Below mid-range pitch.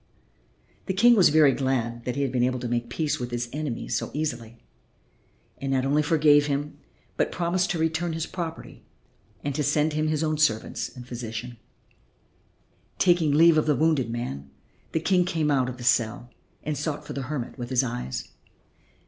No: medium, 145 Hz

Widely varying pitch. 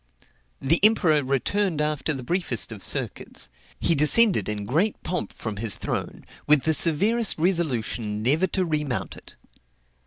Yes: wide, 6.2 semitones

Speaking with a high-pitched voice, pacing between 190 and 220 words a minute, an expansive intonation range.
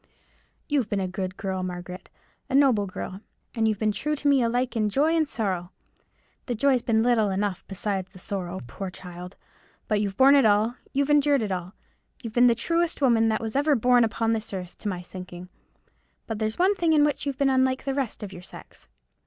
Yes: high, 220 Hz; average, 200 wpm; wide, 5.7 semitones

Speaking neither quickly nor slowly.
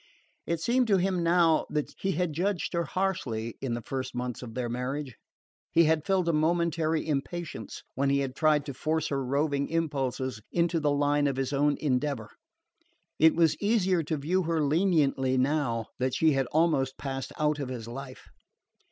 Yes: average, 180 wpm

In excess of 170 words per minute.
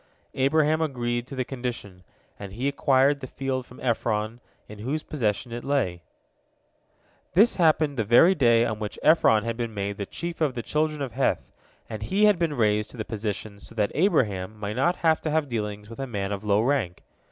Yes: average, 200 wpm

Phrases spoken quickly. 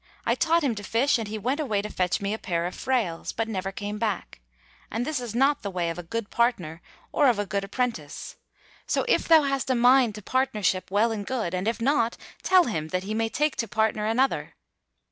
Yes: fast, 230 wpm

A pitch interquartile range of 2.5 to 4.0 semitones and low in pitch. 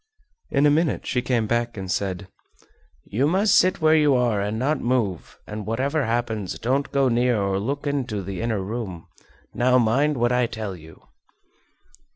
No: average, 4.8 semitones; low, 120 Hz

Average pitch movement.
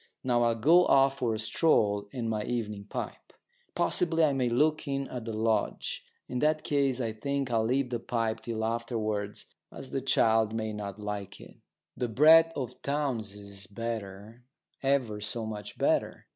Yes: average, 4.0 semitones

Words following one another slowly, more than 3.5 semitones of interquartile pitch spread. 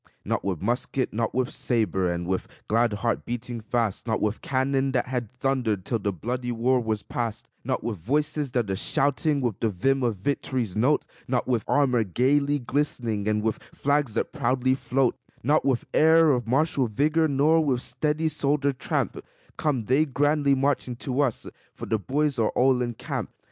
No: average, 180 wpm; average, 3.9 semitones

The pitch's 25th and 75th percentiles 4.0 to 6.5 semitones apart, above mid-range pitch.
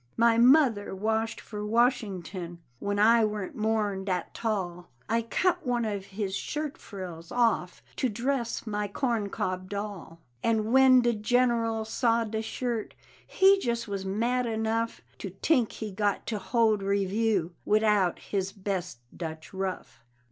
No: average, 3.2 semitones; high, 215 Hz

